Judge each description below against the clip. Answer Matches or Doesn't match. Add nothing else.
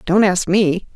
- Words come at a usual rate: Matches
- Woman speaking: Matches